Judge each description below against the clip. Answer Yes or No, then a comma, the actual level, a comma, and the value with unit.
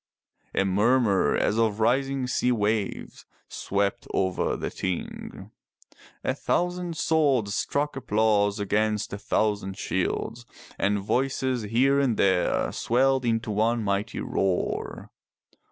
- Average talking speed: No, slow, 120 wpm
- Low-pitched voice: Yes, low, 110 Hz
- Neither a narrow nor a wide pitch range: Yes, average, 4.2 semitones